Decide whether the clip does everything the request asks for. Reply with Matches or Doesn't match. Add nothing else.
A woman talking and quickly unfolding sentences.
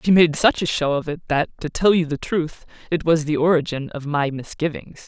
Matches